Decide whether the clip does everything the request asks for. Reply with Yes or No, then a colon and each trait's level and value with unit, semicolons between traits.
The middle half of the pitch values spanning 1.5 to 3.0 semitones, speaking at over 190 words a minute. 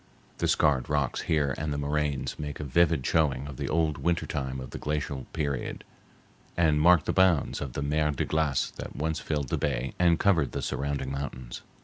Yes: narrow, 2.4 semitones; average, 200 wpm